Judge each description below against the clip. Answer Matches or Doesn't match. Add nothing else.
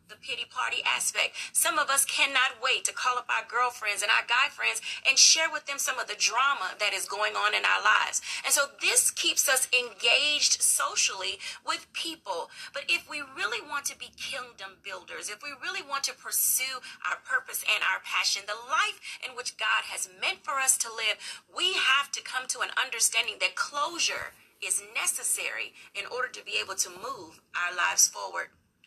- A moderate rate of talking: Matches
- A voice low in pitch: Doesn't match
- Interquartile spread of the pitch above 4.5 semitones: Matches